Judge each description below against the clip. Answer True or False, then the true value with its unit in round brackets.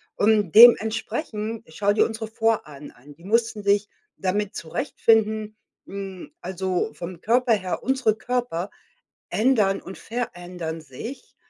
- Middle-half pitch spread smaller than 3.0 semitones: False (3.5 semitones)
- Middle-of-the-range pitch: False (210 Hz)